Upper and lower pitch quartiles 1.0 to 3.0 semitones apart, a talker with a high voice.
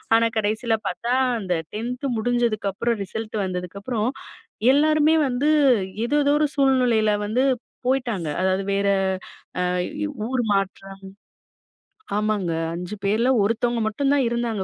No: average, 3.9 semitones; high, 225 Hz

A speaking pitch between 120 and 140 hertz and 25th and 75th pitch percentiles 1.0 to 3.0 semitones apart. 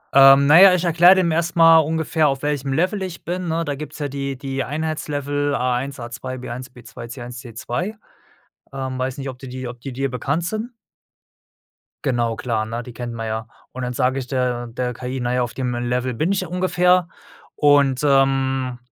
No: low, 135 Hz; average, 4.1 semitones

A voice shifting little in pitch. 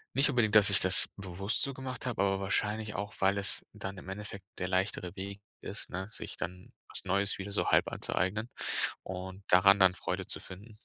Yes: narrow, 1.9 semitones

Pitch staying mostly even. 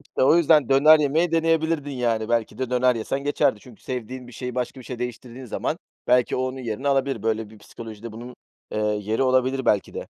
No: average, 3.1 semitones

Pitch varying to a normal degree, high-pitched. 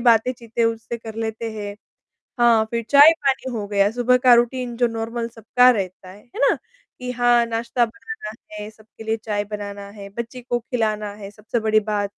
No: narrow, 2.2 semitones; high, 225 Hz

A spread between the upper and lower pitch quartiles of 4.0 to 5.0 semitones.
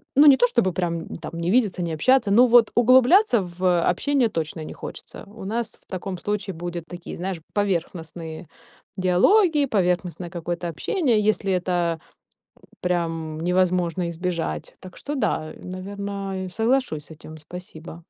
Yes: average, 4.3 semitones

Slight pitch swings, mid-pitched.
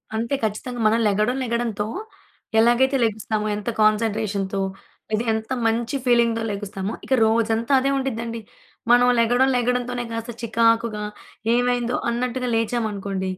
No: narrow, 2.2 semitones; high, 230 Hz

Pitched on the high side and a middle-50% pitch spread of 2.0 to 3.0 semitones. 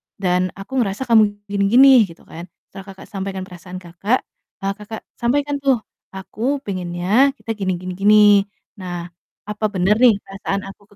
No: high, 200 Hz; average, 3.6 semitones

